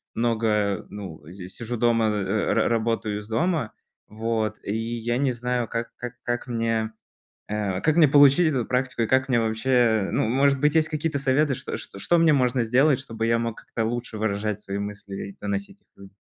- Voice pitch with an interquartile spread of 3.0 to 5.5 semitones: Yes, average, 3.5 semitones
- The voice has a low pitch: Yes, low, 115 Hz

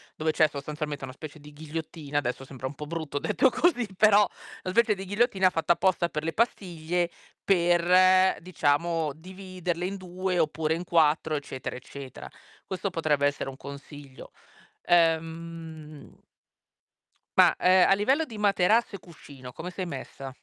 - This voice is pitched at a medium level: Yes, medium, 165 Hz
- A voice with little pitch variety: No, average, 3.8 semitones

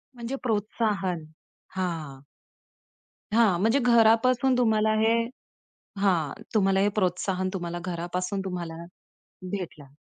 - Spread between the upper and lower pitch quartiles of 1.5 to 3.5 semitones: No, average, 4.1 semitones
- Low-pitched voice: No, high, 195 Hz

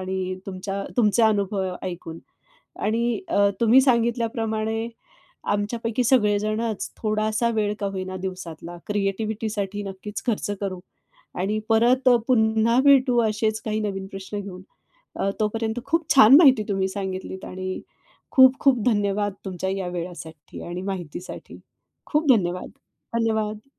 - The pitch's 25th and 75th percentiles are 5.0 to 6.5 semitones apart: No, average, 3.1 semitones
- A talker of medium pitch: No, high, 210 Hz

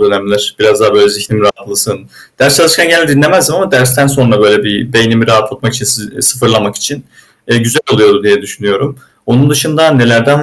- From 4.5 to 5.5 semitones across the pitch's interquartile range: Yes, average, 5.1 semitones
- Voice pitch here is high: No, low, 125 Hz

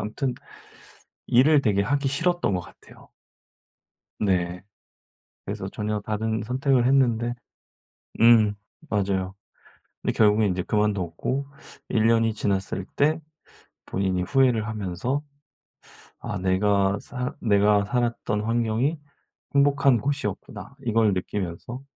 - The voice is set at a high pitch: No, low, 110 Hz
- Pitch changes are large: No, average, 4.2 semitones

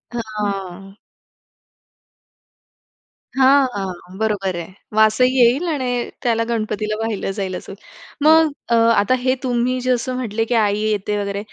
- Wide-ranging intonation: No, average, 3.7 semitones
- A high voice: Yes, high, 225 Hz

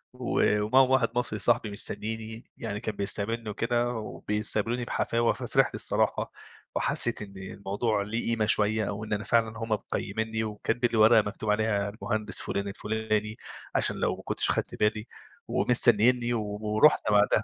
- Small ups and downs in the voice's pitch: Yes, narrow, 1.8 semitones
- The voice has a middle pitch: No, low, 110 Hz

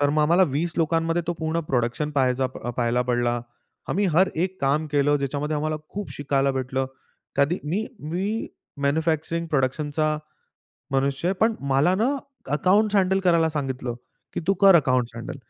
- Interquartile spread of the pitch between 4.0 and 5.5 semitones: Yes, average, 4.3 semitones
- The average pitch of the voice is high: No, medium, 150 Hz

